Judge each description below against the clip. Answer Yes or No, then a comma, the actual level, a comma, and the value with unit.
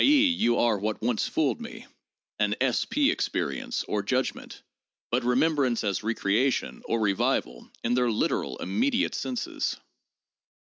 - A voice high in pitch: No, low, 125 Hz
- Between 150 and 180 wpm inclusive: No, slow, 135 wpm